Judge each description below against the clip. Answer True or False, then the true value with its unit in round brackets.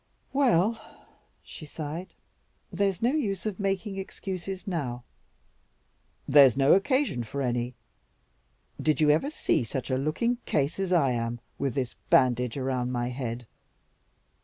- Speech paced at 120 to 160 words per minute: True (135 wpm)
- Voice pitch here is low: False (150 Hz)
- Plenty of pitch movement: True (7.6 semitones)